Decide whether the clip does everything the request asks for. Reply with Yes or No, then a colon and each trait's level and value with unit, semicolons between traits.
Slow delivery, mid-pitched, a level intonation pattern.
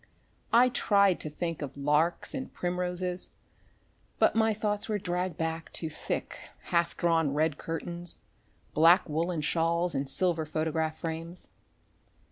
Yes: slow, 130 wpm; medium, 170 Hz; narrow, 2.2 semitones